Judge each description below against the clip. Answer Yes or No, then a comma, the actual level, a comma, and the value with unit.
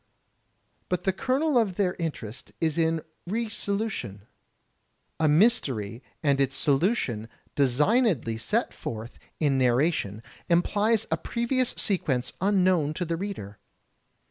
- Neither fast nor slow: No, slow, 115 wpm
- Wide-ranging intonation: Yes, wide, 7.9 semitones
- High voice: No, medium, 165 Hz